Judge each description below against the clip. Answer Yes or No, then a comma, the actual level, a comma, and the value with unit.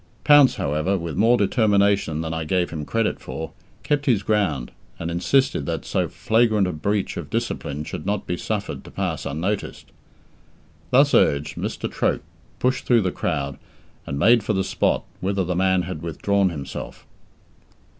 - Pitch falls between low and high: No, very low, 95 Hz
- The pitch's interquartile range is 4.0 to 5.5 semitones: Yes, average, 4.8 semitones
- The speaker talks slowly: No, average, 165 wpm